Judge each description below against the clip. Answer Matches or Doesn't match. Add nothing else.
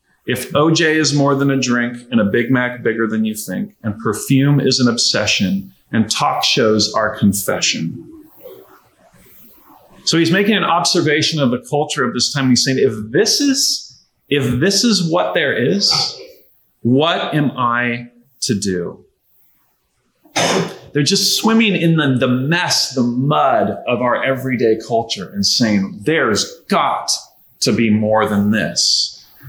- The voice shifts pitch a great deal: Matches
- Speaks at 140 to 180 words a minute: Matches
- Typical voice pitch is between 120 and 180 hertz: Matches